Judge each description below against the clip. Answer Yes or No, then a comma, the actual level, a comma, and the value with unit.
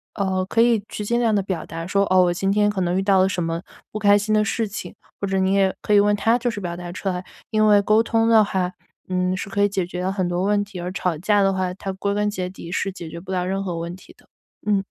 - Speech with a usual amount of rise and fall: No, narrow, 2.2 semitones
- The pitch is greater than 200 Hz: No, high, 195 Hz